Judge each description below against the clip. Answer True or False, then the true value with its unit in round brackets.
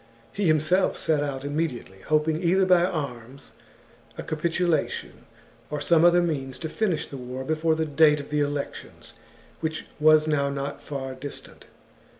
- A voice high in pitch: False (155 Hz)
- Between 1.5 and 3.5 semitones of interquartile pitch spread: True (2.7 semitones)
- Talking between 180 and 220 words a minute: False (155 wpm)